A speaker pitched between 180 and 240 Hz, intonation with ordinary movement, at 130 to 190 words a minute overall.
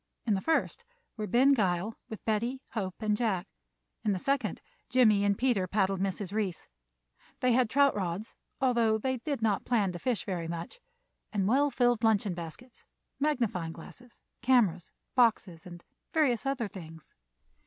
Yes: high, 215 Hz; average, 4.8 semitones; average, 155 wpm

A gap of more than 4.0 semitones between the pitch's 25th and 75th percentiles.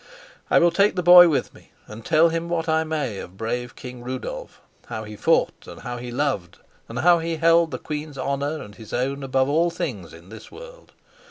Yes: wide, 5.5 semitones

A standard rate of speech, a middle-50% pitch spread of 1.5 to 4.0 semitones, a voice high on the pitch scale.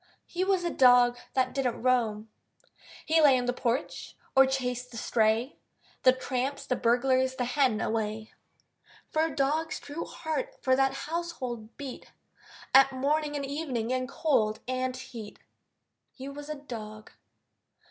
Yes: average, 145 wpm; average, 2.9 semitones; very high, 260 Hz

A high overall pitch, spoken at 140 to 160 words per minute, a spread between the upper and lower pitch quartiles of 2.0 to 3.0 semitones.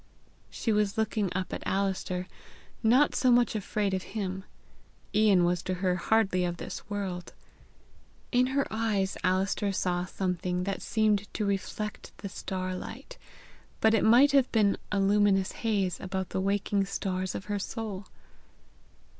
Yes: high, 200 Hz; average, 145 wpm; narrow, 2.5 semitones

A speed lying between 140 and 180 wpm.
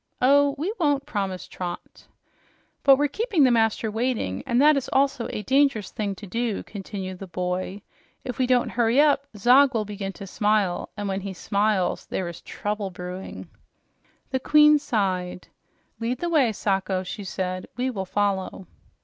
Yes: average, 165 wpm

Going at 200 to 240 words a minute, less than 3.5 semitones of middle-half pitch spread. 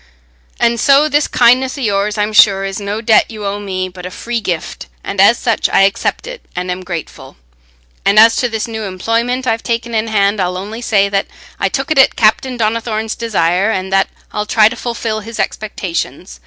Yes: fast, 205 wpm; average, 3.0 semitones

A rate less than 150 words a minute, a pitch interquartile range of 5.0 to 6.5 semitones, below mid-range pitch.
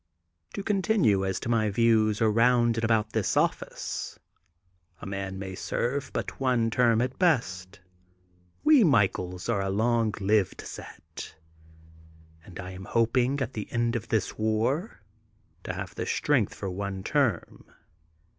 No: average, 140 wpm; average, 3.7 semitones; low, 110 Hz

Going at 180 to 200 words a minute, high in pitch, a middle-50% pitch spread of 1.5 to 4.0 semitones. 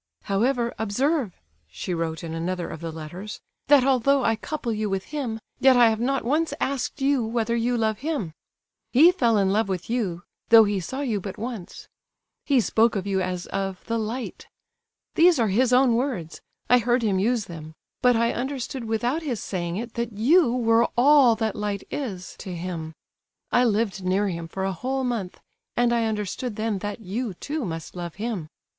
No: average, 190 wpm; high, 225 Hz; average, 4.6 semitones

